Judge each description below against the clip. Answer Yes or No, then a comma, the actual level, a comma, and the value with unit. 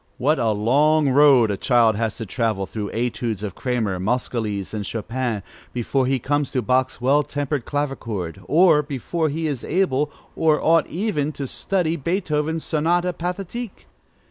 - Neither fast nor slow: Yes, average, 155 wpm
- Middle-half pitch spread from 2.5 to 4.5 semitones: No, average, 5.2 semitones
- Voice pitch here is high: No, low, 135 Hz